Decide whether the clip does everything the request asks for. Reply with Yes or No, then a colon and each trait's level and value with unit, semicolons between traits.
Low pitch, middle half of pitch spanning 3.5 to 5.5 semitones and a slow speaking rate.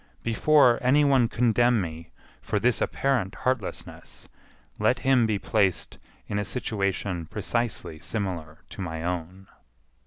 Yes: low, 105 Hz; average, 5.2 semitones; slow, 125 wpm